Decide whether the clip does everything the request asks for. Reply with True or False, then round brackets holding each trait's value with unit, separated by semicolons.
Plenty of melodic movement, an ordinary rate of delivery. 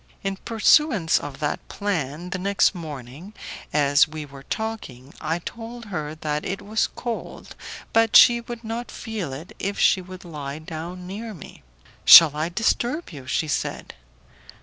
True (6.7 semitones; 160 wpm)